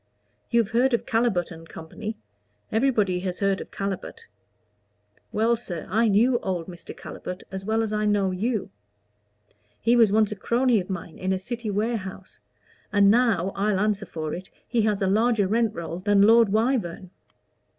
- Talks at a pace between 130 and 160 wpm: No, average, 170 wpm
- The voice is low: No, high, 205 Hz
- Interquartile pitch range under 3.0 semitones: No, average, 3.3 semitones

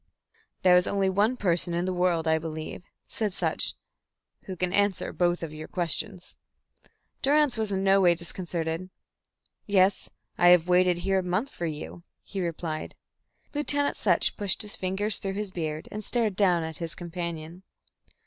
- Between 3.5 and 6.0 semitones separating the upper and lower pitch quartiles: No, average, 2.9 semitones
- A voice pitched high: No, medium, 180 Hz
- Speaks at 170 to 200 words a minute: No, average, 160 wpm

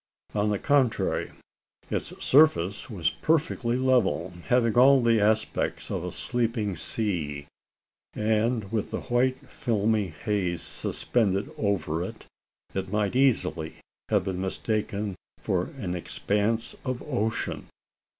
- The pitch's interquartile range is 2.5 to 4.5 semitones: Yes, average, 4.2 semitones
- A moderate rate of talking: No, slow, 120 wpm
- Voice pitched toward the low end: Yes, low, 110 Hz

